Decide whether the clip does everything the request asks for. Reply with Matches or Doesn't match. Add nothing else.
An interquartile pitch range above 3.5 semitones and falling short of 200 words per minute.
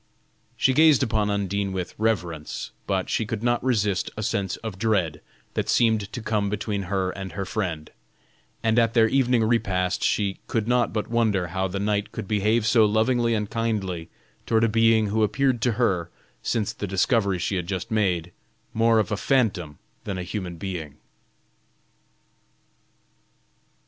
Doesn't match